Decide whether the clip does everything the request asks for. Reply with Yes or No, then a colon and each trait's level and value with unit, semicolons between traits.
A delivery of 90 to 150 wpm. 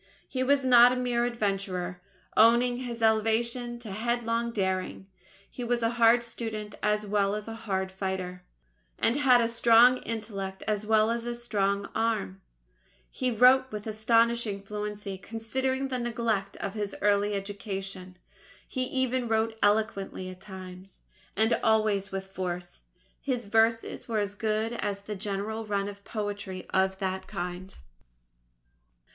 Yes: average, 140 wpm